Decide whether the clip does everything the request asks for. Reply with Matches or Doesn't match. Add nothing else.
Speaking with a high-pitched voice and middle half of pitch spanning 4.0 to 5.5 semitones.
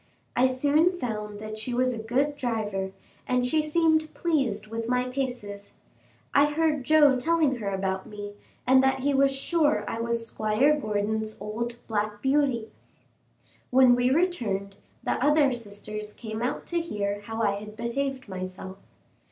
Matches